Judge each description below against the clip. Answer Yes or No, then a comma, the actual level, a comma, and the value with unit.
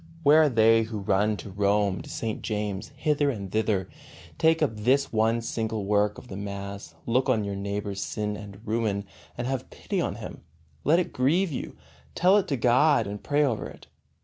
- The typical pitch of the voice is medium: No, low, 110 Hz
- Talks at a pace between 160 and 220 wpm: Yes, average, 195 wpm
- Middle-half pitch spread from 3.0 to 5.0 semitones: Yes, average, 4.5 semitones